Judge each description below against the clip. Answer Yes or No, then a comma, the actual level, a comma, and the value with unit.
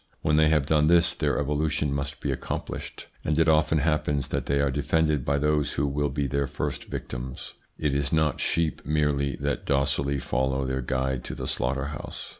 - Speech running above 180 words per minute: Yes, average, 195 wpm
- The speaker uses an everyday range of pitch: No, narrow, 1.8 semitones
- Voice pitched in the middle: No, very low, 70 Hz